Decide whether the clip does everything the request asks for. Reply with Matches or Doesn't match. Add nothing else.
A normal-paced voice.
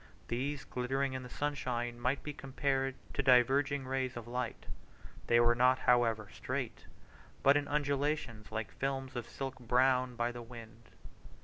Matches